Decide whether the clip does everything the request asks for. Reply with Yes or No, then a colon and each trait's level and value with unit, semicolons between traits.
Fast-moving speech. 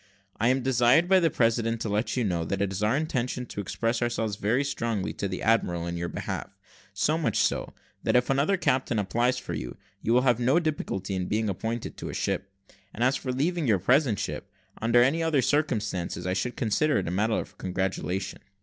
Yes: fast, 215 wpm